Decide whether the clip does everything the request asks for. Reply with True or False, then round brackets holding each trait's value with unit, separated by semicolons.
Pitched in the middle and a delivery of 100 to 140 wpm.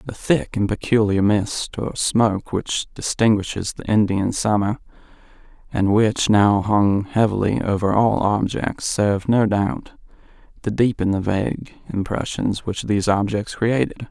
False (105 Hz; 135 wpm)